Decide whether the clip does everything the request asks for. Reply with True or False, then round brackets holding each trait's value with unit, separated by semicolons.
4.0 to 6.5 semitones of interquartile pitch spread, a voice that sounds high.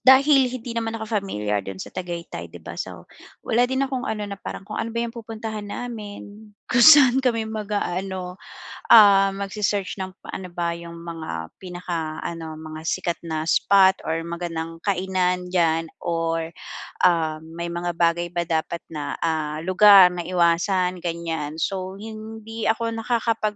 False (4.6 semitones; 180 Hz)